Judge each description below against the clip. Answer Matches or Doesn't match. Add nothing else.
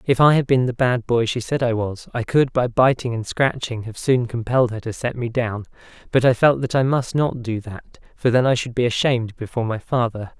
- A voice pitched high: Doesn't match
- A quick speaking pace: Matches